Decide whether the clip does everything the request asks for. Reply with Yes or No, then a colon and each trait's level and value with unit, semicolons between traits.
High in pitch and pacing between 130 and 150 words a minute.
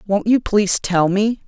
No: high, 205 Hz; fast, 205 wpm